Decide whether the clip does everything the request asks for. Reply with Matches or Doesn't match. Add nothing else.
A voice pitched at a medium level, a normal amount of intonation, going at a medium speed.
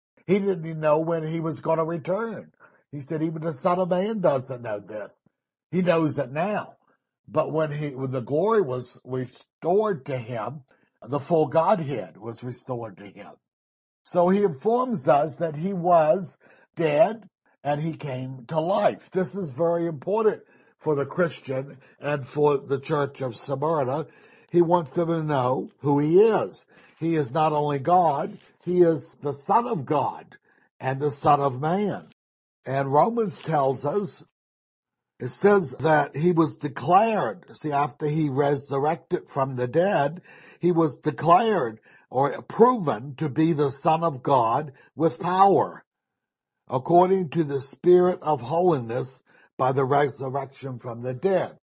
Matches